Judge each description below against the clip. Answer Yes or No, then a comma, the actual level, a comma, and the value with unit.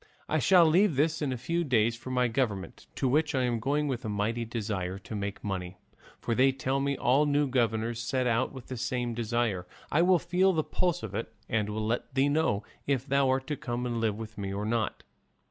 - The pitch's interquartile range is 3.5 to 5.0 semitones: Yes, average, 4.0 semitones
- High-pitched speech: No, low, 125 Hz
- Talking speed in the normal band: No, fast, 230 wpm